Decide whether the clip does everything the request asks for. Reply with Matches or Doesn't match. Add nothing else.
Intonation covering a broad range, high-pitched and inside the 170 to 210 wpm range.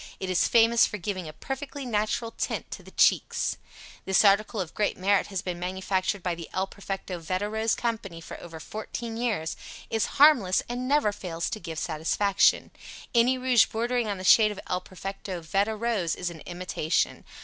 Doesn't match